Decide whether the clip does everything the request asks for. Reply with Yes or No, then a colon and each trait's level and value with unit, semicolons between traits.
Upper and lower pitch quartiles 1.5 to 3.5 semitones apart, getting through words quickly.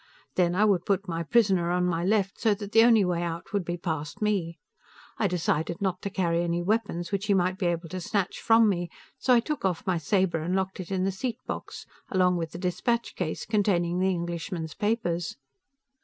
Yes: average, 2.9 semitones; fast, 215 wpm